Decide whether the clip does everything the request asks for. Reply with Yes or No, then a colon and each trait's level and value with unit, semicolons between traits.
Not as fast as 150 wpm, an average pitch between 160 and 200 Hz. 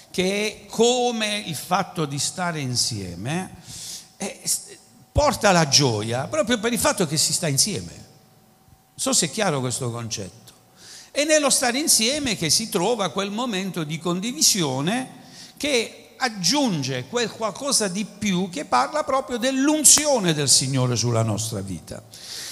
Yes: average, 140 wpm; high, 190 Hz